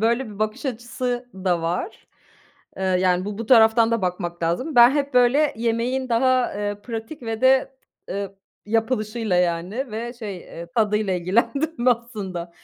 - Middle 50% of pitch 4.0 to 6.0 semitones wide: Yes, average, 4.4 semitones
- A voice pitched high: Yes, high, 225 Hz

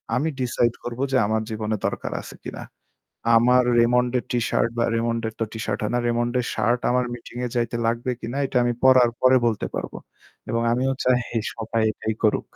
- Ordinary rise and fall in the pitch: No, narrow, 1.6 semitones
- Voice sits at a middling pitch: No, low, 120 Hz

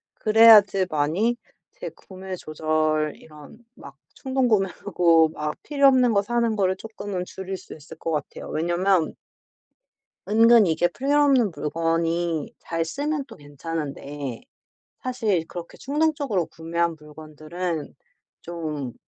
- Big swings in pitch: Yes, wide, 6.1 semitones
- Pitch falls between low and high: Yes, medium, 175 Hz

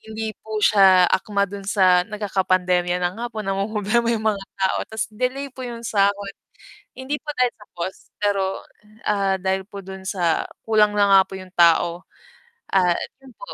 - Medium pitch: No, high, 200 Hz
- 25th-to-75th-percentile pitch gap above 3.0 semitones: No, narrow, 2.5 semitones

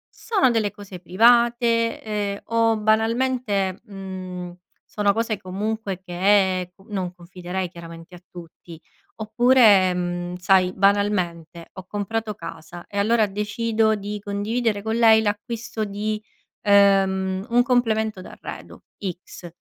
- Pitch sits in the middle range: No, high, 205 Hz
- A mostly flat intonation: No, average, 3.2 semitones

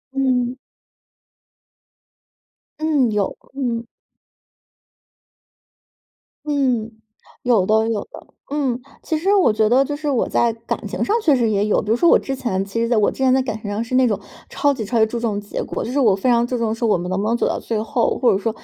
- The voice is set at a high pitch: Yes, high, 235 Hz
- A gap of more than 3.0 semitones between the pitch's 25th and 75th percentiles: Yes, average, 3.4 semitones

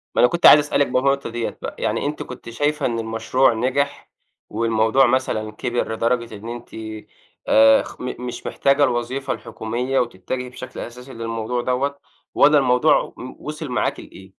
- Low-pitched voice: Yes, low, 125 Hz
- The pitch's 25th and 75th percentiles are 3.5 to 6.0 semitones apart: No, average, 3.0 semitones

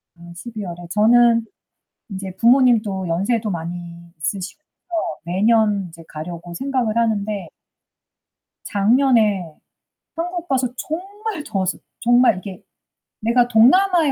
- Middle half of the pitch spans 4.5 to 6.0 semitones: Yes, wide, 5.4 semitones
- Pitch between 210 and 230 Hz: Yes, high, 215 Hz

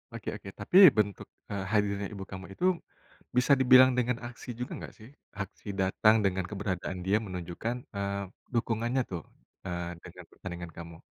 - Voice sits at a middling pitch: No, low, 100 Hz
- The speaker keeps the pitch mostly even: No, average, 3.8 semitones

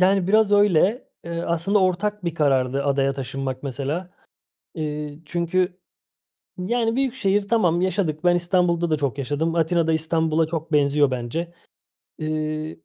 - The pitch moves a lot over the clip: No, average, 3.8 semitones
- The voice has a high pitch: No, medium, 165 Hz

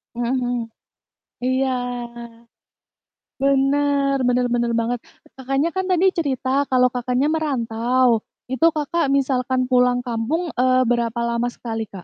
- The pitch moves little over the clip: Yes, narrow, 2.3 semitones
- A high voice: Yes, very high, 255 Hz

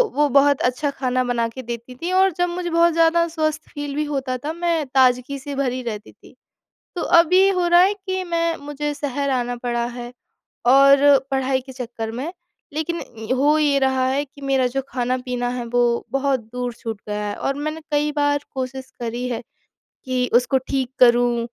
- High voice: Yes, very high, 270 Hz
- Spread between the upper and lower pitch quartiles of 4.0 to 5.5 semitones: No, average, 3.3 semitones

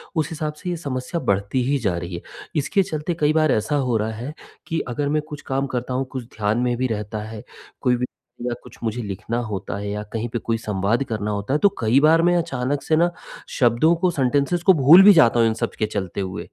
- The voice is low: Yes, low, 125 Hz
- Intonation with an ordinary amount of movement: No, wide, 5.9 semitones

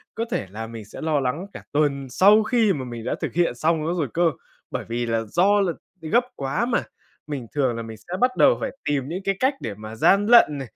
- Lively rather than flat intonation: Yes, wide, 8.3 semitones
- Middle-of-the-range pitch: Yes, medium, 150 Hz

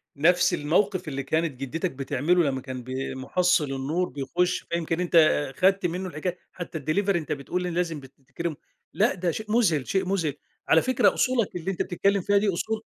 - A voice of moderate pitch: Yes, medium, 170 Hz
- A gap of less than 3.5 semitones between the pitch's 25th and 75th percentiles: No, average, 4.3 semitones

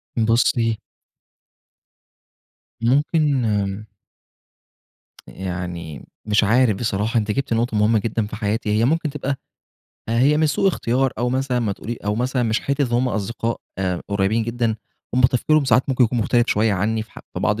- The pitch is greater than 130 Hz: No, low, 115 Hz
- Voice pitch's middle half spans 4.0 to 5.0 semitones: No, average, 3.3 semitones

